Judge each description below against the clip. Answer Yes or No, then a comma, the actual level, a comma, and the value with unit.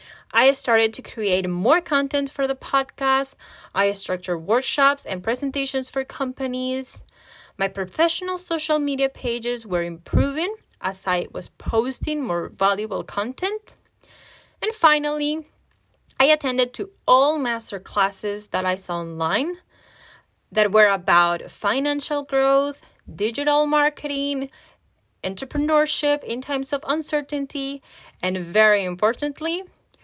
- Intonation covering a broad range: Yes, wide, 6.1 semitones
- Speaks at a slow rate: Yes, slow, 115 wpm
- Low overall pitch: No, very high, 265 Hz